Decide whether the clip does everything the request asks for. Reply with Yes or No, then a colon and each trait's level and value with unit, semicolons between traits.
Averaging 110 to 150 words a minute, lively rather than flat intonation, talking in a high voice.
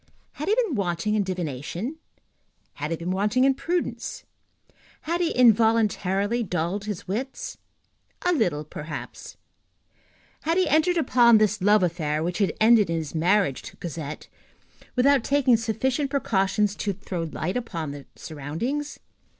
Yes: average, 140 wpm; wide, 7.0 semitones; high, 205 Hz